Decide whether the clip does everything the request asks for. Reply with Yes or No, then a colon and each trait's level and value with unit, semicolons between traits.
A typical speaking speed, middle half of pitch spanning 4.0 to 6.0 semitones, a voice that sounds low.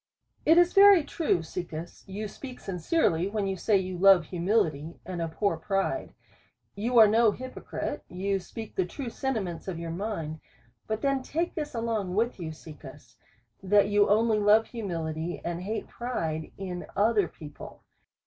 No: average, 160 wpm; average, 4.8 semitones; high, 195 Hz